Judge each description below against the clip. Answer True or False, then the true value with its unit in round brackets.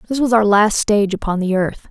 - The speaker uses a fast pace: True (250 wpm)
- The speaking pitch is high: True (210 Hz)